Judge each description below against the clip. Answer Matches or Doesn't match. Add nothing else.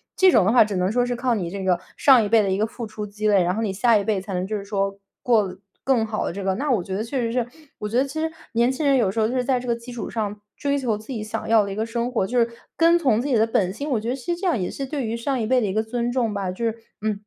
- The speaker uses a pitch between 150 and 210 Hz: Doesn't match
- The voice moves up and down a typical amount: Matches